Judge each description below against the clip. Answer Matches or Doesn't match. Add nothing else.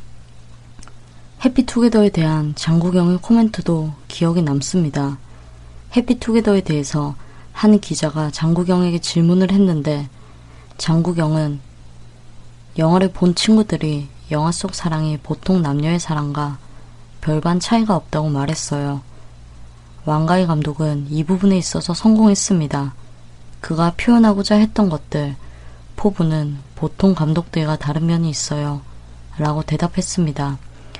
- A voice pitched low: Doesn't match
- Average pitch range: Matches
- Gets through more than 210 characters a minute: Matches